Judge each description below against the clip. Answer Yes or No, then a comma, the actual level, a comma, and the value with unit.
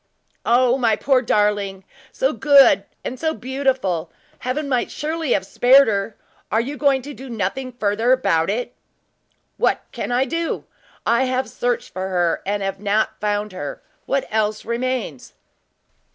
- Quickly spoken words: No, average, 155 wpm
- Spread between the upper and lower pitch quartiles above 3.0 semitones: Yes, average, 4.4 semitones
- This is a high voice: Yes, high, 240 Hz